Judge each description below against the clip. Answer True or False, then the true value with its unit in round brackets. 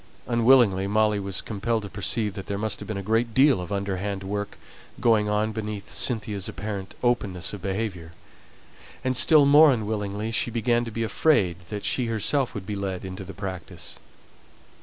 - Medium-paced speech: True (175 wpm)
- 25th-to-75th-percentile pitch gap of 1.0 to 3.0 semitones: True (2.7 semitones)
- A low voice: True (105 Hz)